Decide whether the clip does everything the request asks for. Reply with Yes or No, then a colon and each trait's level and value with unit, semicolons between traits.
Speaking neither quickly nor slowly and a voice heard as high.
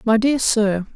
Yes: average, 190 wpm; high, 225 Hz